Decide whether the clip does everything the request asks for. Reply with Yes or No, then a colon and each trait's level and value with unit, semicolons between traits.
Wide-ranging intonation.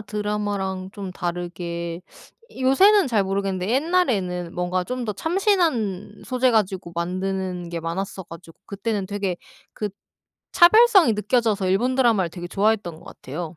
No: average, 4.8 semitones